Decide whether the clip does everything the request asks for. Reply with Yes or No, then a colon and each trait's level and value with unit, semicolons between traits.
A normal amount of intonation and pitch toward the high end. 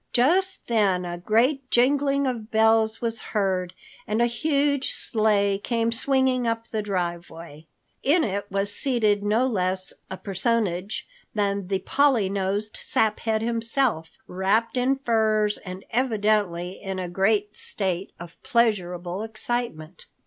Yes: average, 3.8 semitones; high, 215 Hz